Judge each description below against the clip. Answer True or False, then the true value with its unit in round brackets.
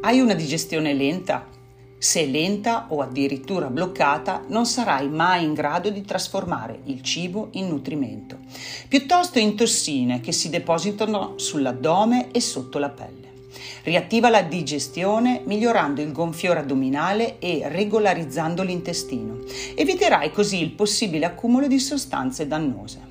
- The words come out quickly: False (125 wpm)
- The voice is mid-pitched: True (170 Hz)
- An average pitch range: False (7.2 semitones)